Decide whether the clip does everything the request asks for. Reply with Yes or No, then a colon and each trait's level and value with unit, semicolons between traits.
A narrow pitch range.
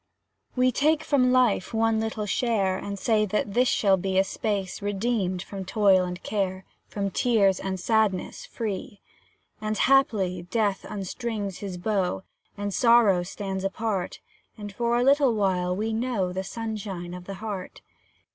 No: average, 3.0 semitones